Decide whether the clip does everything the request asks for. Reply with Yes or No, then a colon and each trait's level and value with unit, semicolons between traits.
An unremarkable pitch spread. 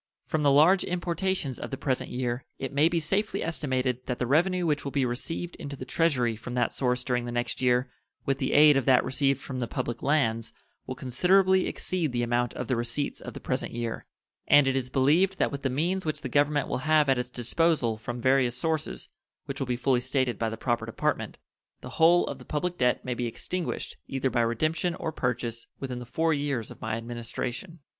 Yes: average, 4.2 semitones